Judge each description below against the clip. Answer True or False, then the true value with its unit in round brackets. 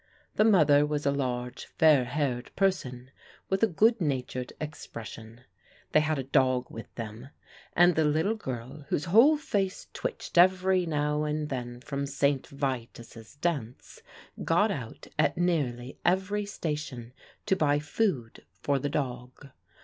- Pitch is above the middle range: False (145 Hz)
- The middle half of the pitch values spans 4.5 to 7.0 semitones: True (5.5 semitones)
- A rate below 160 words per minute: True (140 wpm)